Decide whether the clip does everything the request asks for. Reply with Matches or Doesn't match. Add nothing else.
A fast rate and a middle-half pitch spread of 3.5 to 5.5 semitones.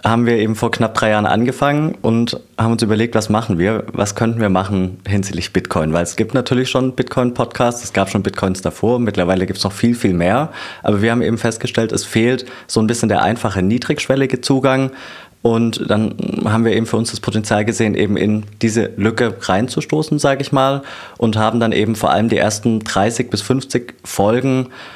Doesn't match